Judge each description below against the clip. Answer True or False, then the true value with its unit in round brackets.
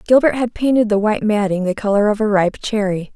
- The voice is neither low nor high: False (210 Hz)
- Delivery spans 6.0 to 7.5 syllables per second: True (6.1 syllables/s)